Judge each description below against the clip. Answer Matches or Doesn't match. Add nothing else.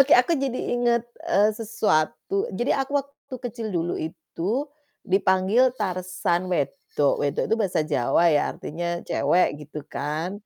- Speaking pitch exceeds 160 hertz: Matches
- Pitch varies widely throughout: Matches